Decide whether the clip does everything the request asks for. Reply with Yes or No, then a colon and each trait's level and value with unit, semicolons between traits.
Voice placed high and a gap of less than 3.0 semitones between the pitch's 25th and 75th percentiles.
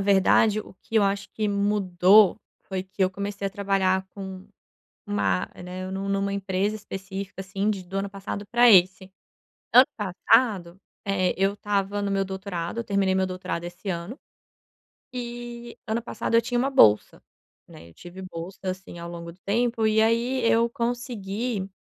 Yes: high, 195 Hz; narrow, 2.5 semitones